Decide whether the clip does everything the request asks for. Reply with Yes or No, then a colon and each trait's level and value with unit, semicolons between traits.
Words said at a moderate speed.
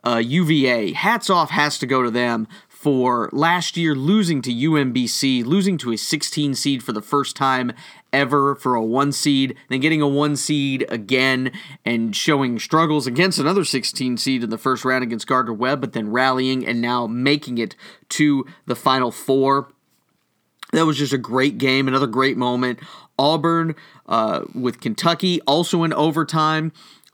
Yes: average, 170 wpm